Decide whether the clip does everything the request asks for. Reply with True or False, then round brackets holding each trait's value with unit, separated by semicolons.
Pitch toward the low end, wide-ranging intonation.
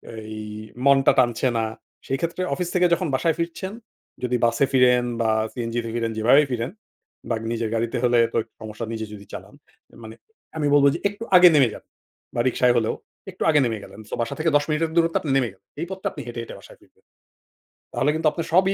True (125 Hz; 6.0 semitones)